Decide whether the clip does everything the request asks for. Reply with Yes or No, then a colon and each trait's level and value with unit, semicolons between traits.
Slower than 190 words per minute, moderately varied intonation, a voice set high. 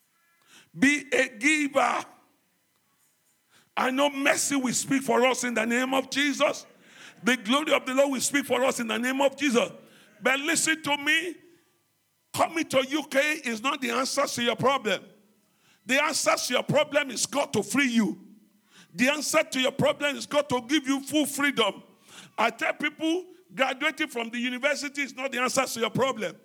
Yes: average, 180 wpm; average, 3.1 semitones; very high, 275 Hz